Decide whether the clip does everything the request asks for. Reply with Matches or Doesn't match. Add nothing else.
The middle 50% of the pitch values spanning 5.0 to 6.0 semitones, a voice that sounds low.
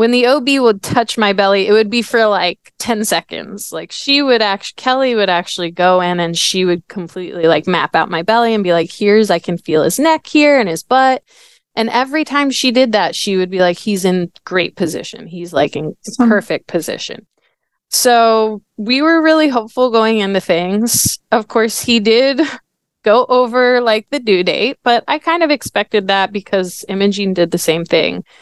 Doesn't match